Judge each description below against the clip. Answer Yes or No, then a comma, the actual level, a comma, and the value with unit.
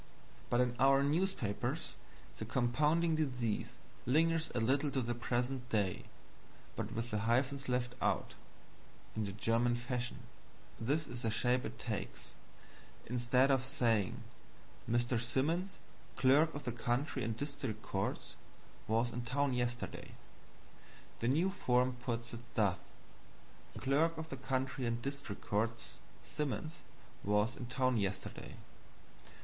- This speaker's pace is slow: Yes, slow, 130 wpm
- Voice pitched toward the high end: No, low, 125 Hz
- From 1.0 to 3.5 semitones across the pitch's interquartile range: Yes, average, 3.0 semitones